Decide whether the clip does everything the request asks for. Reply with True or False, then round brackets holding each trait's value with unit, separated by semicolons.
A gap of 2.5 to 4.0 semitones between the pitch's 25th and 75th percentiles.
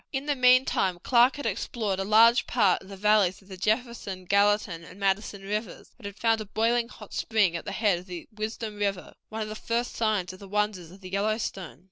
True (2.8 semitones)